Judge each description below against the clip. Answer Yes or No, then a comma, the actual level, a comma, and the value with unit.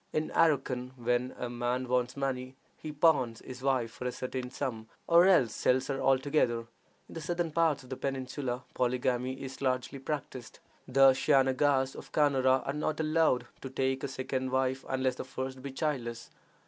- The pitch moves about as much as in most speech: No, narrow, 1.8 semitones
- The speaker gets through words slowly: No, average, 175 wpm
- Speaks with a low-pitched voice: Yes, low, 130 Hz